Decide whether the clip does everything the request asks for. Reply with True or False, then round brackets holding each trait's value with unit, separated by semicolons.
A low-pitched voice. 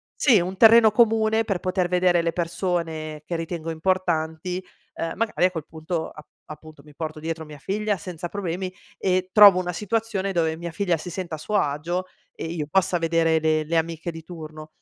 False (170 Hz)